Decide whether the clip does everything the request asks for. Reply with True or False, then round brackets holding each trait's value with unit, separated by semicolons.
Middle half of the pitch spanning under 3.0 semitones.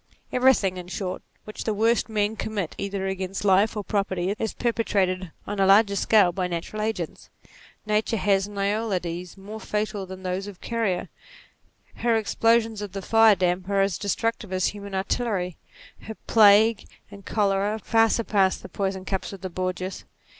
True (2.5 semitones)